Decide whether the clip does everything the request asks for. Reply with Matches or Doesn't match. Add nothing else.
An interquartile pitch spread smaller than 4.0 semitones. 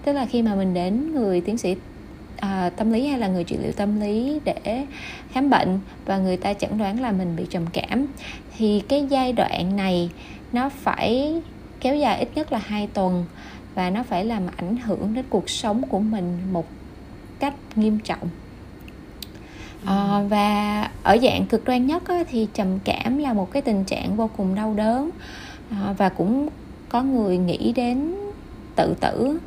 Doesn't match